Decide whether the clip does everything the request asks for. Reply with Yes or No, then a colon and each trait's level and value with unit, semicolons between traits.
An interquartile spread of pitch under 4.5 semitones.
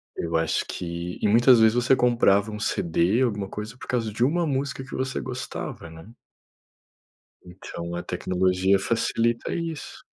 No: average, 5.3 semitones